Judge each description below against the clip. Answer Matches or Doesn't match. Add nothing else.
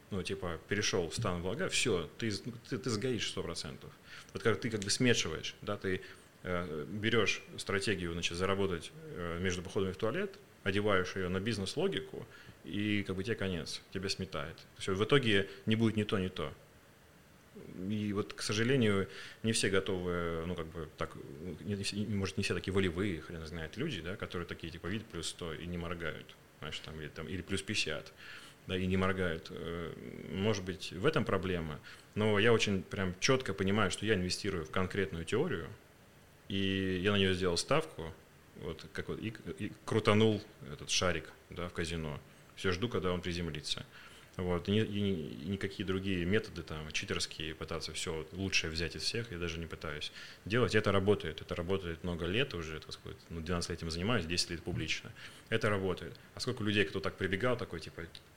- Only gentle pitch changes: Doesn't match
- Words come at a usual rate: Doesn't match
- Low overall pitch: Matches